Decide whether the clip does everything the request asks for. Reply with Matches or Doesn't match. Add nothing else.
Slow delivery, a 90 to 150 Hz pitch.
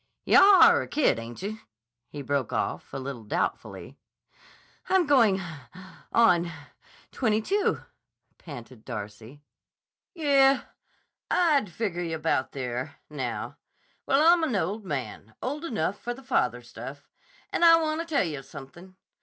Doesn't match